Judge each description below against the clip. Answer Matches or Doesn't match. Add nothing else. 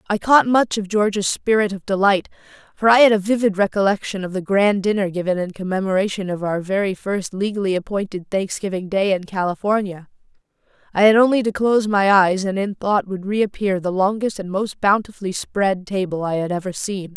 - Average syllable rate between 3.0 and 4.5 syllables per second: Doesn't match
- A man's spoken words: Doesn't match